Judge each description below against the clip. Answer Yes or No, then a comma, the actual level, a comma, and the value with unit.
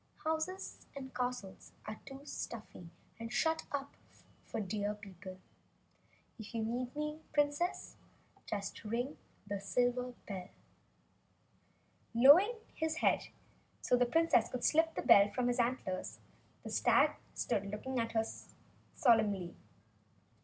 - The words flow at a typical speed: No, slow, 125 wpm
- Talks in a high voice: Yes, high, 245 Hz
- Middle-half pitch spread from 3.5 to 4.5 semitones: No, wide, 5.5 semitones